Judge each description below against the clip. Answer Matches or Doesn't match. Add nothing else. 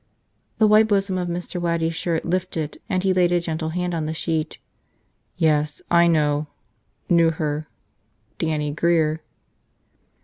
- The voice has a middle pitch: Matches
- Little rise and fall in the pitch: Matches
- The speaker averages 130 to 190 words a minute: Matches